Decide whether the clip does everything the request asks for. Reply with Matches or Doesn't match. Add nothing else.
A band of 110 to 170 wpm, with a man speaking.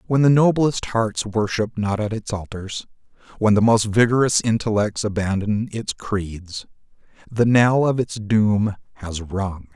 Matches